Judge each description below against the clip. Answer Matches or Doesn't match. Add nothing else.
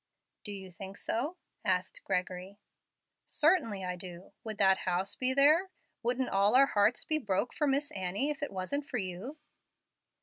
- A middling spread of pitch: Doesn't match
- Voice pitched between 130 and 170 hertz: Doesn't match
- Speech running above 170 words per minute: Doesn't match